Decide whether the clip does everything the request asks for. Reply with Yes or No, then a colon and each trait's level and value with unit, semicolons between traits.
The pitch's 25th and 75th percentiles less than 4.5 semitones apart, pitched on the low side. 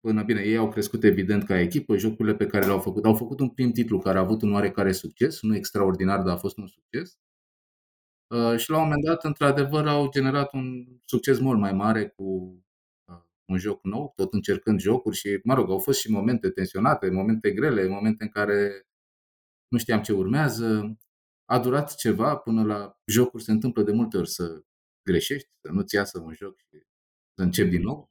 Yes: average, 4.1 semitones; low, 110 Hz